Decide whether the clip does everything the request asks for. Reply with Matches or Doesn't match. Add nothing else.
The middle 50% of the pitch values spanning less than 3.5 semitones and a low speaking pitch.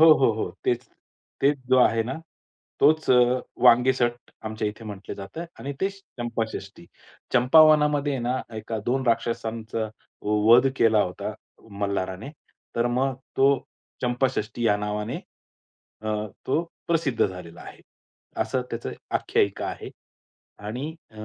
Doesn't match